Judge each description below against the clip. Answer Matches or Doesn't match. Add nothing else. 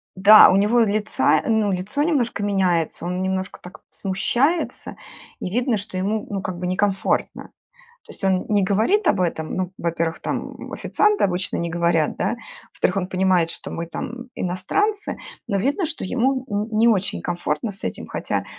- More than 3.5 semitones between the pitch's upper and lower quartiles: Matches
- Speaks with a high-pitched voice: Matches